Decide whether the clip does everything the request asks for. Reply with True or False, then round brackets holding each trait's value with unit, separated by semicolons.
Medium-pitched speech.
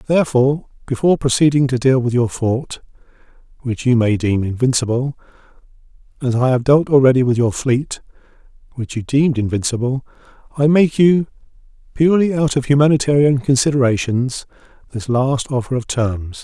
False (130 Hz)